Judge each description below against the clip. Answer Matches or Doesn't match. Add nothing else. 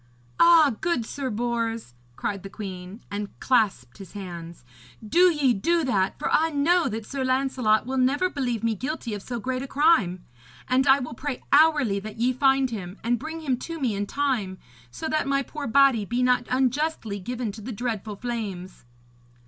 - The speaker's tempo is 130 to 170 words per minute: Doesn't match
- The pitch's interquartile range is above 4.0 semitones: Matches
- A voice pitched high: Matches